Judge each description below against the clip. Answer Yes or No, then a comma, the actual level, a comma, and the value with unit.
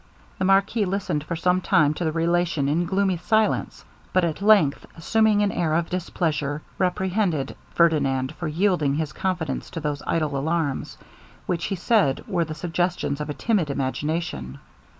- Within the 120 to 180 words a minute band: Yes, average, 160 wpm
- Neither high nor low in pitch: Yes, medium, 170 Hz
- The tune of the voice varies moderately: Yes, average, 3.8 semitones